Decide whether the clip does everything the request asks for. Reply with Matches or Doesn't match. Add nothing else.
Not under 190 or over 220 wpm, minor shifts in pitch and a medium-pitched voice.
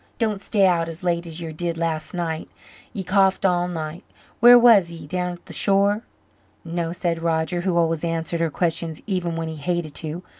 Matches